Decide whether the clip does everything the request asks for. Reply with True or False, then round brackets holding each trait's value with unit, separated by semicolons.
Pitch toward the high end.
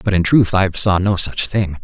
False (95 Hz)